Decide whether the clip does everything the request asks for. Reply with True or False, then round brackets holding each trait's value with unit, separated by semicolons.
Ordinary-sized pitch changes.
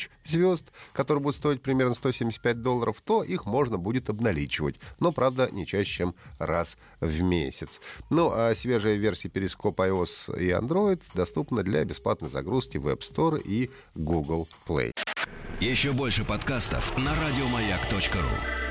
False (6.9 semitones)